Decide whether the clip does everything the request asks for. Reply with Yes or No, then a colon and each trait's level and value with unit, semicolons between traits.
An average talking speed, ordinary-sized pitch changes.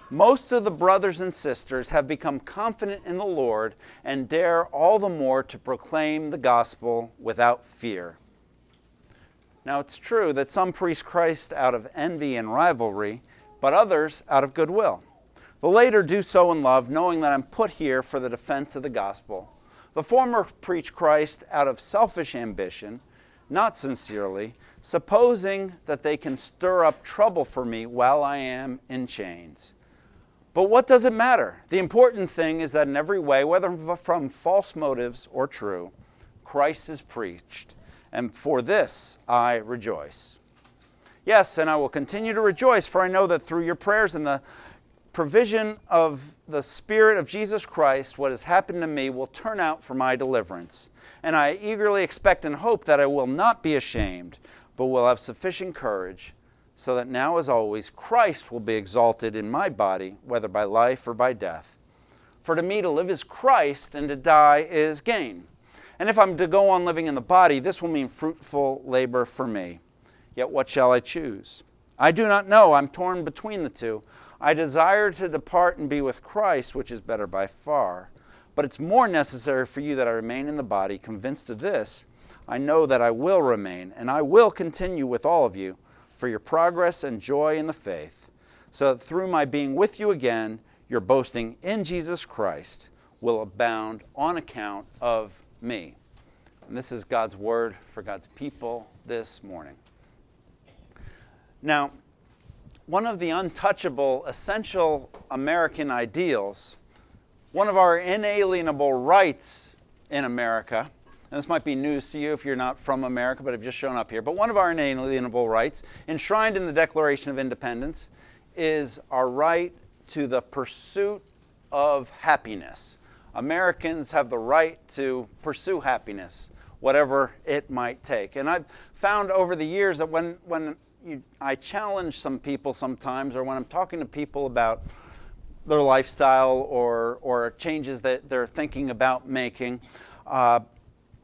No: average, 170 wpm; wide, 6.0 semitones